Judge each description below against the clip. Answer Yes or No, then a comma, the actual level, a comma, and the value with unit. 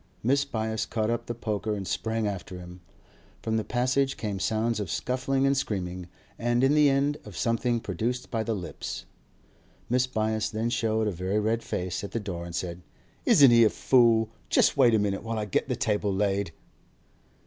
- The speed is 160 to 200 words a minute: Yes, average, 190 wpm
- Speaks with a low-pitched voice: Yes, low, 110 Hz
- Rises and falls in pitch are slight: No, average, 3.0 semitones